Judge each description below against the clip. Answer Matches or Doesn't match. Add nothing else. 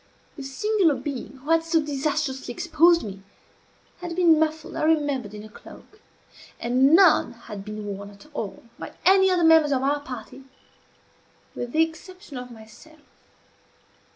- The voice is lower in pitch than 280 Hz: Doesn't match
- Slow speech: Doesn't match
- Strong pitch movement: Doesn't match